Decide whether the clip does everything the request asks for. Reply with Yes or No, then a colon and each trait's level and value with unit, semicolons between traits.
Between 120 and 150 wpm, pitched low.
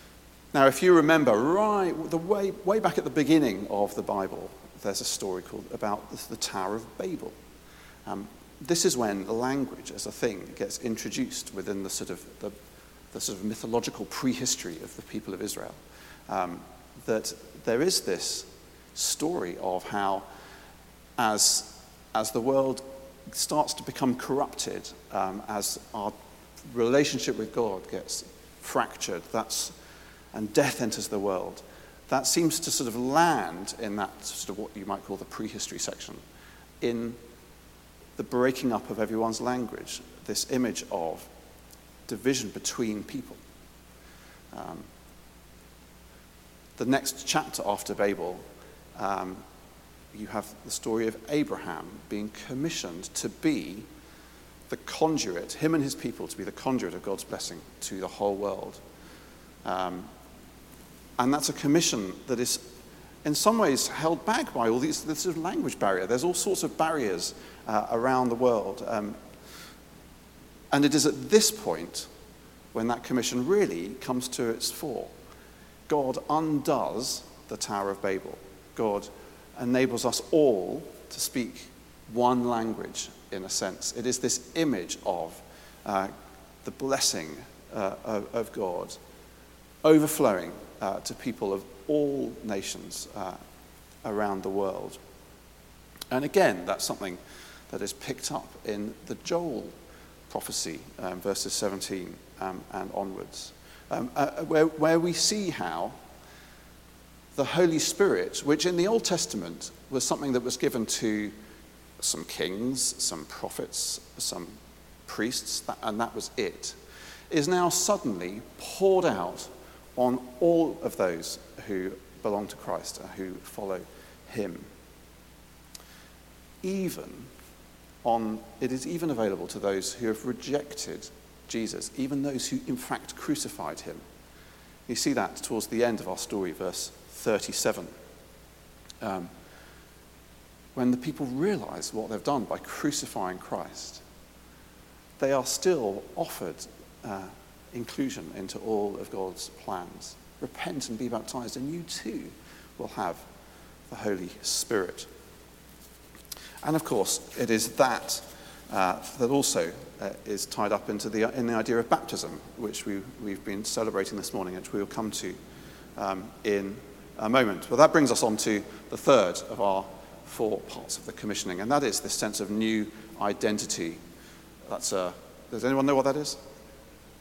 Yes: average, 145 wpm; low, 115 Hz